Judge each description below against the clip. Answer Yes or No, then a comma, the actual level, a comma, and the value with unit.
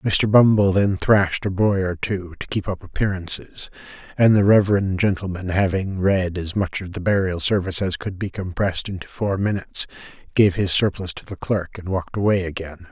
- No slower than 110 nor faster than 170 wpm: No, average, 190 wpm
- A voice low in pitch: Yes, very low, 95 Hz